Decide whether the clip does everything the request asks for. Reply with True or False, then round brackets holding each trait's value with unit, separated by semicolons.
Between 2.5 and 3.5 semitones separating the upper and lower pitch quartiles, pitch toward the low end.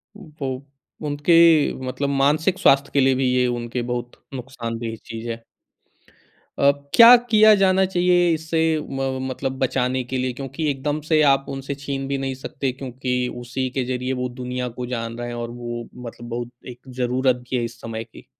True (3.0 semitones; 130 Hz)